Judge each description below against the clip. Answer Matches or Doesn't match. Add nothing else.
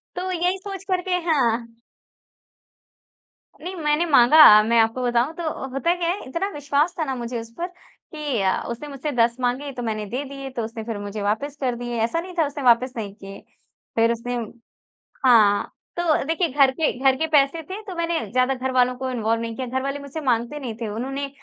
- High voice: Matches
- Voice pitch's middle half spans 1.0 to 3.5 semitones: Doesn't match